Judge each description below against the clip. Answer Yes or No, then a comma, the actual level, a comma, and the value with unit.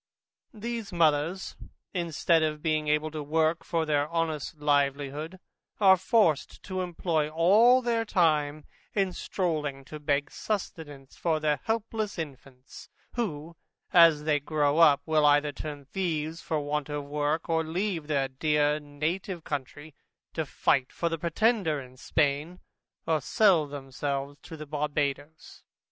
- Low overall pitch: No, medium, 155 Hz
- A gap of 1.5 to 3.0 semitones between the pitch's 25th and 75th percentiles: Yes, average, 2.7 semitones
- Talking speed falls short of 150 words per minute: Yes, slow, 135 wpm